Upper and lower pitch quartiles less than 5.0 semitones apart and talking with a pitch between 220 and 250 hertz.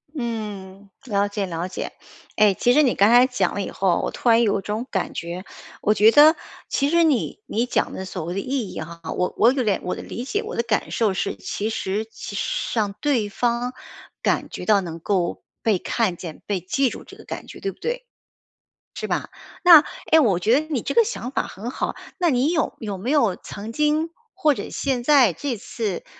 No: wide, 5.5 semitones; high, 225 Hz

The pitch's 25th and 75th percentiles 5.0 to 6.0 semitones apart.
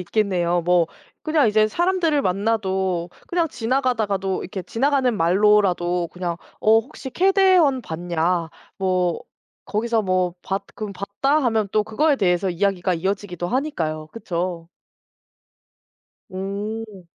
No: average, 4.6 semitones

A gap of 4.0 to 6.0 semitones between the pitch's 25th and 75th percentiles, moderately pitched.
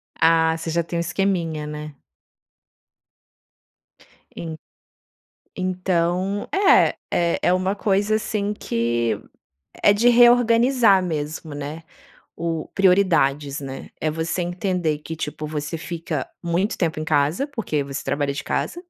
Yes: average, 4.3 semitones; medium, 170 Hz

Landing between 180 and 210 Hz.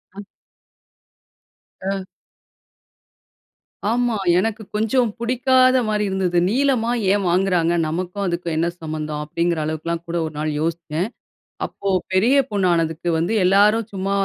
Yes: high, 190 Hz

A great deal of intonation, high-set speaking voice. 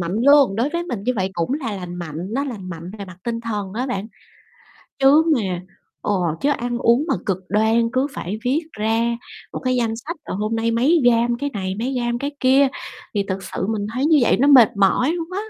No: average, 4.9 semitones; high, 235 Hz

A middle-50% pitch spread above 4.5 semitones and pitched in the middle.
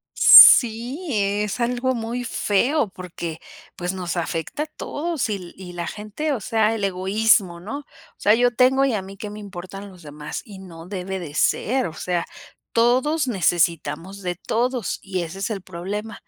No: average, 4.9 semitones; high, 200 Hz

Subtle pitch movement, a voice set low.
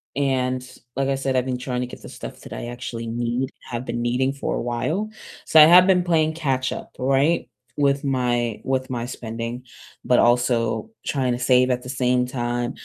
Yes: narrow, 2.1 semitones; low, 125 Hz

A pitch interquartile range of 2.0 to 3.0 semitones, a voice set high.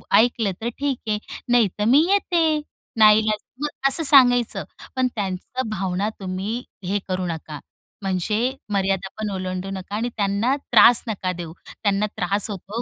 No: average, 4.2 semitones; high, 210 Hz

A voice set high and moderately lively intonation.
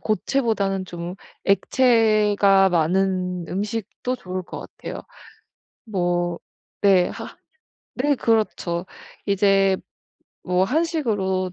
Yes: high, 195 Hz; average, 3.1 semitones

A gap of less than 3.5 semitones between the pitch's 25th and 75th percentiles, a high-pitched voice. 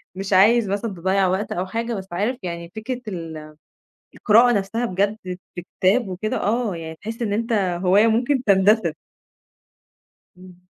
No: average, 3.8 semitones; high, 200 Hz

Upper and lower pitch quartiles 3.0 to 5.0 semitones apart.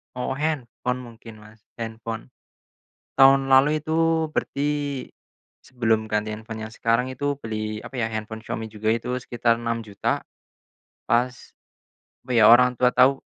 No: narrow, 2.4 semitones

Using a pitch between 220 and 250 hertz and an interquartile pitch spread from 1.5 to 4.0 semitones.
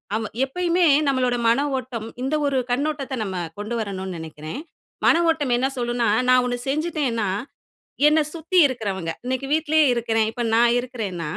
No: high, 245 Hz; average, 4.4 semitones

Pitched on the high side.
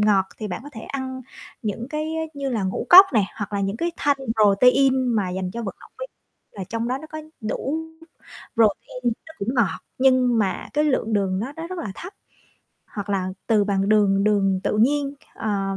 Yes: high, 220 Hz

